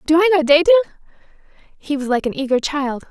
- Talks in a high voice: Yes, very high, 315 Hz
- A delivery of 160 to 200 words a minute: Yes, average, 195 wpm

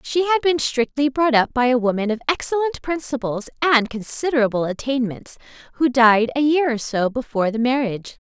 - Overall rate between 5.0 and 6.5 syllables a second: Yes, 5.5 syllables/s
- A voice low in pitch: No, very high, 255 Hz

